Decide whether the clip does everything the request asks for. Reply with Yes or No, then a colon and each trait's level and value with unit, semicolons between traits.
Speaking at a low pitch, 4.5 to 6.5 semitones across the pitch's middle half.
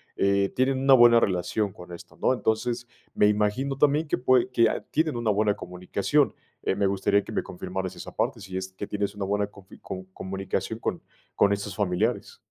No: low, 105 Hz; average, 3.8 semitones